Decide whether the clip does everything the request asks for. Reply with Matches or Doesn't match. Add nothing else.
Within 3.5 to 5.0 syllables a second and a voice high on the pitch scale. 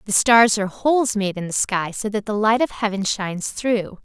Doesn't match